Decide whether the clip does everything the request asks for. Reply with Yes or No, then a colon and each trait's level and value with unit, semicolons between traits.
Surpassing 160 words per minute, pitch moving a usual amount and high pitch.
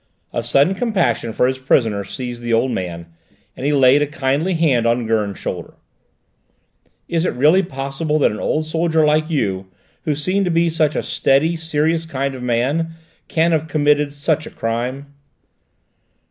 No: average, 170 wpm; average, 4.5 semitones; medium, 145 Hz